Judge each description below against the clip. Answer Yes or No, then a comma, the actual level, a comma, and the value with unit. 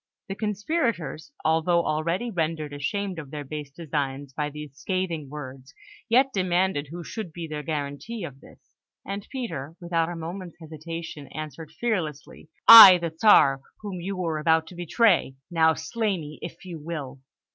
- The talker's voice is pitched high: No, medium, 165 Hz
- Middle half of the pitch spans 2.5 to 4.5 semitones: Yes, average, 3.7 semitones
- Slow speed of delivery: No, average, 155 wpm